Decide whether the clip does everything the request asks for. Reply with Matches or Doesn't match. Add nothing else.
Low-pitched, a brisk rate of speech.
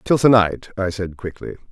Matches